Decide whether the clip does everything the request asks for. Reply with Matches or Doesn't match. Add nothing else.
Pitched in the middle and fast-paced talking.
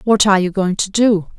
Doesn't match